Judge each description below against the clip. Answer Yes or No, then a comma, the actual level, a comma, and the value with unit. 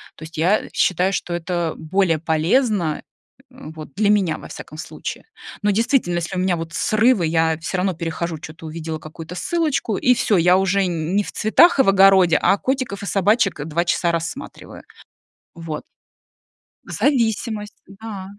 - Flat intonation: No, average, 4.1 semitones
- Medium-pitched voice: Yes, medium, 180 Hz